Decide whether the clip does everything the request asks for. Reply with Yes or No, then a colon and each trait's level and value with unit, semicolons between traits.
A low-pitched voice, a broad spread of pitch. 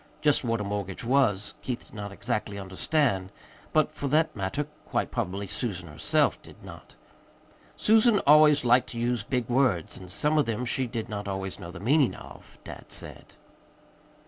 Yes: low, 115 Hz; wide, 5.9 semitones